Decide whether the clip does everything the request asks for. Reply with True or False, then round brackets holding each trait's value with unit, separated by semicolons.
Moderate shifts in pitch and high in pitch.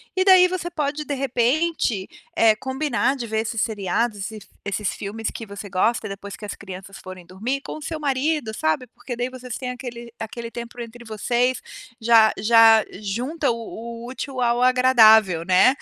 True (3.4 semitones; 235 Hz)